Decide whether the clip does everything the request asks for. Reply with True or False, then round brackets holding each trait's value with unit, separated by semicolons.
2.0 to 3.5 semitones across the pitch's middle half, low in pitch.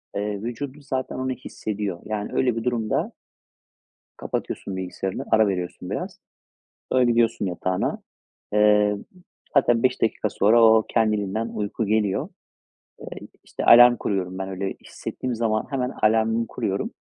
True (2.8 semitones; 110 Hz)